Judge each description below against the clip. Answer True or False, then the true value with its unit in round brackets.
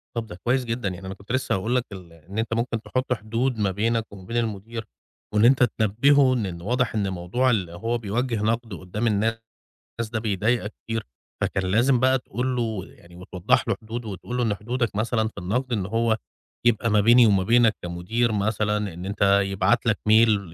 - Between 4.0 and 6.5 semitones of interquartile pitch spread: False (3.2 semitones)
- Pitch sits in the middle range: False (110 Hz)